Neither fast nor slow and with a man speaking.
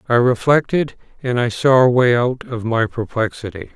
Yes: average, 175 wpm; male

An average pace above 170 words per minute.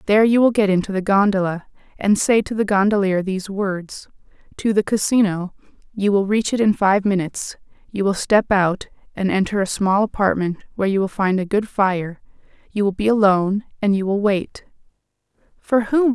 Yes: average, 185 wpm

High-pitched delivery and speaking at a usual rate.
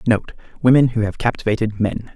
No: low, 110 Hz; average, 165 wpm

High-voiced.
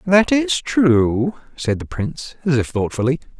No: medium, 150 Hz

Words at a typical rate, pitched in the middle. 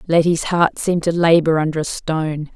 Yes: average, 190 wpm; medium, 165 Hz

